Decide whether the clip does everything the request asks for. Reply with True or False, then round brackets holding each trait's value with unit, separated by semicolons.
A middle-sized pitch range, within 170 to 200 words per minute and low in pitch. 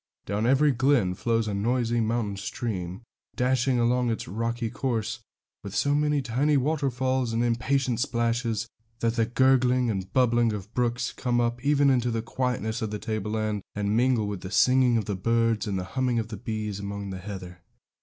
True (3.0 semitones; 180 wpm; 115 Hz)